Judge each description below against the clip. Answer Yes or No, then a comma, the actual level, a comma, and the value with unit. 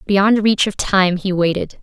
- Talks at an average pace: Yes, average, 195 wpm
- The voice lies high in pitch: Yes, high, 195 Hz